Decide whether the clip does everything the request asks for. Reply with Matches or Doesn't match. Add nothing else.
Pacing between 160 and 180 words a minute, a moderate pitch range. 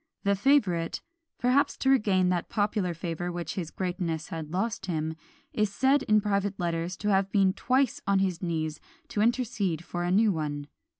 Matches